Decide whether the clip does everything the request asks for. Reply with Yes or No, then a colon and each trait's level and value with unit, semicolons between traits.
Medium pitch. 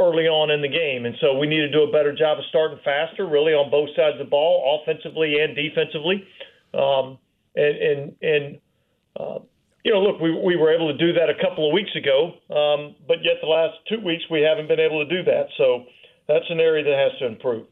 Yes: medium, 160 Hz